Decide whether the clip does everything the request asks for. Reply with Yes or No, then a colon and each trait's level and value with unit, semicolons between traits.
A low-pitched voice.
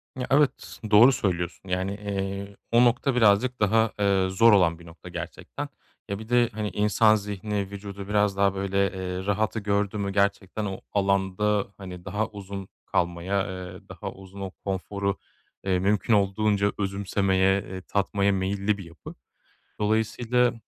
Yes: low, 100 Hz